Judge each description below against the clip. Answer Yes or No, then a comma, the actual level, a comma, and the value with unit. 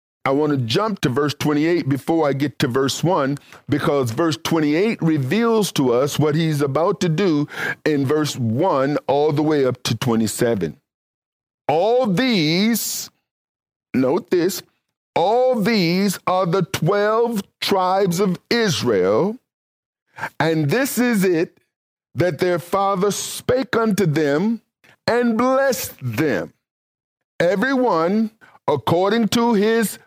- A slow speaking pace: Yes, slow, 125 wpm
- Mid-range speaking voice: Yes, medium, 180 Hz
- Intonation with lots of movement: Yes, wide, 6.7 semitones